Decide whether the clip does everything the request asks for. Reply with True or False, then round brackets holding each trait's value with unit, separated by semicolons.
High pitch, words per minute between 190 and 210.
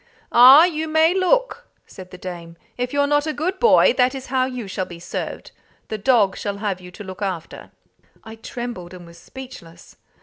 True (240 Hz; 195 wpm)